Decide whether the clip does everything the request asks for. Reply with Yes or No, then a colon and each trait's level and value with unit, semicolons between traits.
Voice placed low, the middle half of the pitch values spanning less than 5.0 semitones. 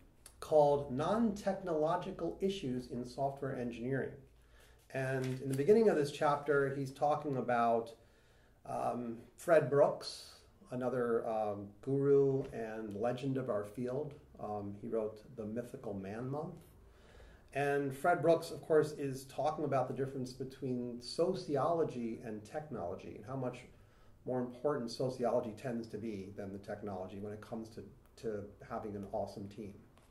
Yes: low, 125 Hz; average, 4.2 semitones